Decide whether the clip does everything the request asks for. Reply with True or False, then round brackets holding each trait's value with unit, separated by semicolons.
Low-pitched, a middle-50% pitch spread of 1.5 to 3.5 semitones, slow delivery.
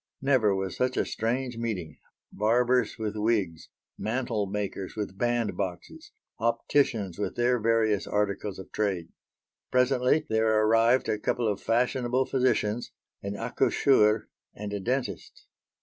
True (110 Hz; 3.2 semitones; 125 wpm)